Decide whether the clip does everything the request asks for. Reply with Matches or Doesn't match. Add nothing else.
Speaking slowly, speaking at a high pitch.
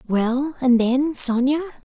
Matches